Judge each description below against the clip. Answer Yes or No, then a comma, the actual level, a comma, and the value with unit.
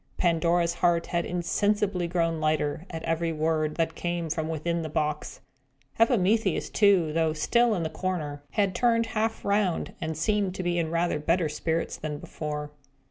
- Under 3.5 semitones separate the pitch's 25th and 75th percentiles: Yes, average, 2.8 semitones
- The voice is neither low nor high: Yes, medium, 170 Hz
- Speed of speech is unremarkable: Yes, average, 165 wpm